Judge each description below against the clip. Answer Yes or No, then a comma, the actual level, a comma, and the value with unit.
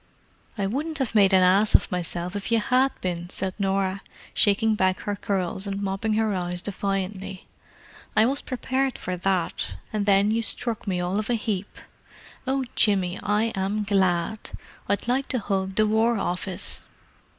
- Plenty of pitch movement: No, average, 2.7 semitones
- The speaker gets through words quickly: No, average, 170 wpm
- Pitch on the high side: Yes, high, 200 Hz